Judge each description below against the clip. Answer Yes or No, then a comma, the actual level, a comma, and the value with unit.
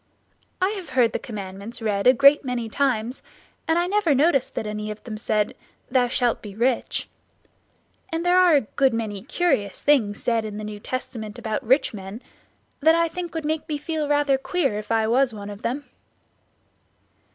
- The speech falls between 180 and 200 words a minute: Yes, average, 185 wpm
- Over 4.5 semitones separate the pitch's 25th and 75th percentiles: Yes, wide, 5.6 semitones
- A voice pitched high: Yes, very high, 250 Hz